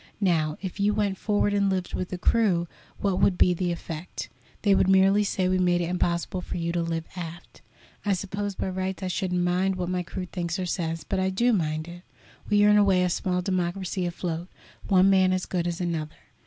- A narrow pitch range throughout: Yes, narrow, 1.8 semitones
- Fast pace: Yes, fast, 220 wpm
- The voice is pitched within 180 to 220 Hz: Yes, medium, 185 Hz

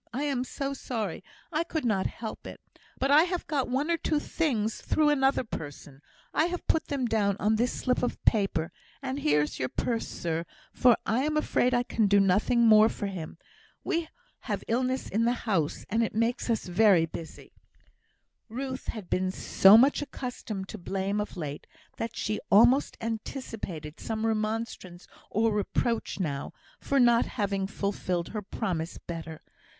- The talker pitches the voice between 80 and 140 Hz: No, high, 225 Hz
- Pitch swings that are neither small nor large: Yes, average, 5.0 semitones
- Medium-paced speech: Yes, average, 170 wpm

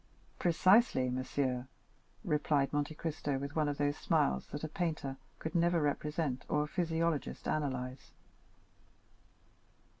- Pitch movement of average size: Yes, average, 3.0 semitones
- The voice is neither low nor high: Yes, medium, 150 Hz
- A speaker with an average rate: No, slow, 120 wpm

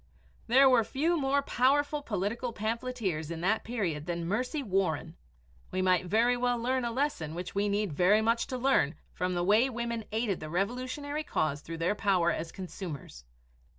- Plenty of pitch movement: Yes, wide, 5.9 semitones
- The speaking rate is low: No, average, 175 wpm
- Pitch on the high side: Yes, high, 215 Hz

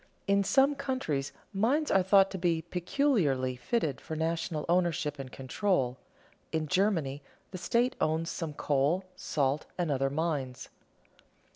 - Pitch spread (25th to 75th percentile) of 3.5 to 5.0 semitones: No, wide, 5.5 semitones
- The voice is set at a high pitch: No, medium, 165 Hz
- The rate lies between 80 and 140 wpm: Yes, slow, 135 wpm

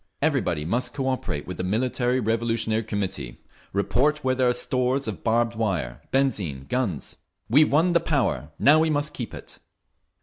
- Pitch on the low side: Yes, low, 120 Hz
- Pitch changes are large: No, average, 4.9 semitones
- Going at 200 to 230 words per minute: No, average, 160 wpm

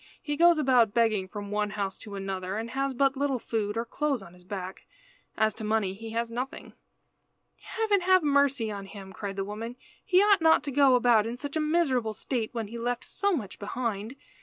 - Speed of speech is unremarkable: No, fast, 210 wpm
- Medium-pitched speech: No, high, 230 Hz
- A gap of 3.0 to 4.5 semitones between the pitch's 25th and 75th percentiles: No, average, 5.1 semitones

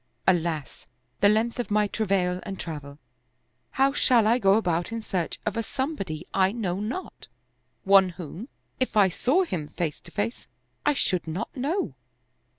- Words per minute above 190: No, average, 165 wpm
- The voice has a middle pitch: No, high, 200 Hz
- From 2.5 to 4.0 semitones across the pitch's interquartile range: No, average, 4.9 semitones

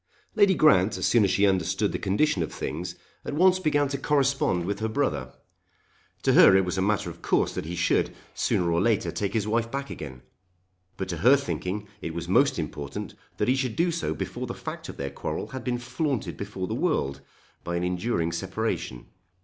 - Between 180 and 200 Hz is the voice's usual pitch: No, low, 100 Hz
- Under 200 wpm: No, fast, 205 wpm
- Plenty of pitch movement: Yes, wide, 7.5 semitones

